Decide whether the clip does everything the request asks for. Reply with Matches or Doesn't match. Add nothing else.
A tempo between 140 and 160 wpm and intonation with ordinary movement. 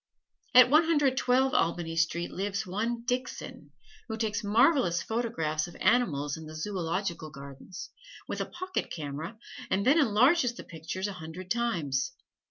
Doesn't match